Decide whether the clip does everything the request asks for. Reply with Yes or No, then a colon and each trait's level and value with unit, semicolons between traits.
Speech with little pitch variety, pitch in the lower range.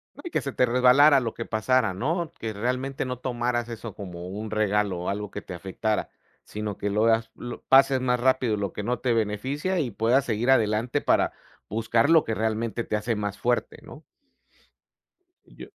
No: average, 3.3 semitones; low, 115 Hz